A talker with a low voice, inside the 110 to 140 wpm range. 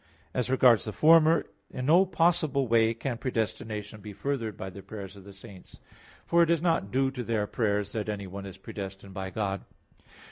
No: low, 110 Hz; average, 185 wpm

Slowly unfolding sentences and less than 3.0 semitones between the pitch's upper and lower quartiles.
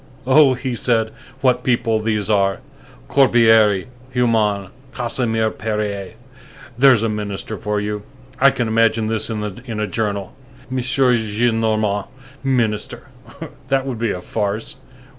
Yes: slow, 125 wpm; narrow, 2.5 semitones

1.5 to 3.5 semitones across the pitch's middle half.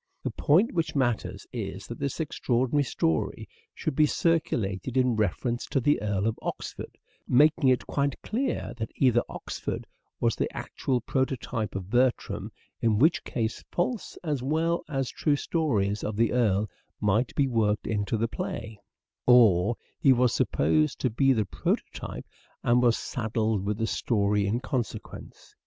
No: average, 4.3 semitones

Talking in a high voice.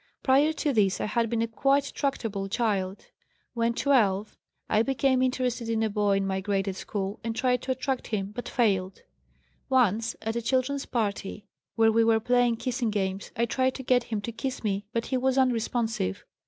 Yes: high, 230 Hz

